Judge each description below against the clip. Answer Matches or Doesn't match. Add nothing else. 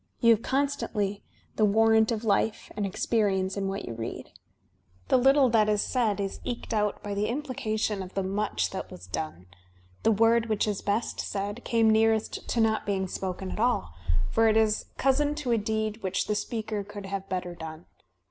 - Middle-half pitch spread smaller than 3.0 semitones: Matches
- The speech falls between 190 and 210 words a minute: Matches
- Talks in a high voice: Matches